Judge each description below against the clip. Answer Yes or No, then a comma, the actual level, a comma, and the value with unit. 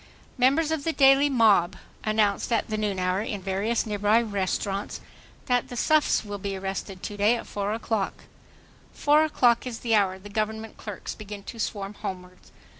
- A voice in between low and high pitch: No, high, 215 Hz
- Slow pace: No, average, 175 wpm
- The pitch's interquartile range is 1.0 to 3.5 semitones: Yes, average, 3.0 semitones